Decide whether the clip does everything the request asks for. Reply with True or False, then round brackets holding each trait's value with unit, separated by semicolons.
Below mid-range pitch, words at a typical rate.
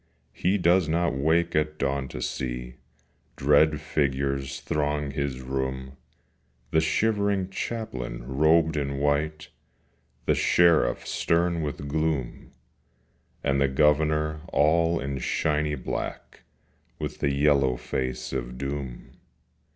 False (75 Hz; 110 wpm)